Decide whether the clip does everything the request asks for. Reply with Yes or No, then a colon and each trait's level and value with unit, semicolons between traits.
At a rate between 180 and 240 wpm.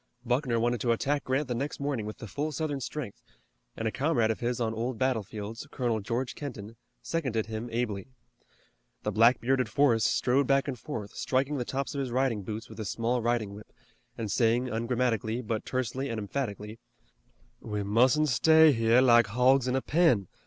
Yes: average, 185 wpm